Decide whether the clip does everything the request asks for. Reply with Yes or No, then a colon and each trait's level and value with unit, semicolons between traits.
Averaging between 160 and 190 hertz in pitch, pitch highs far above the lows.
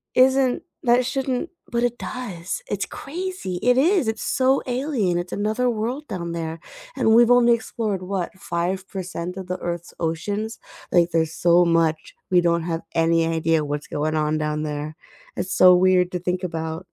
Yes: medium, 185 Hz; wide, 6.3 semitones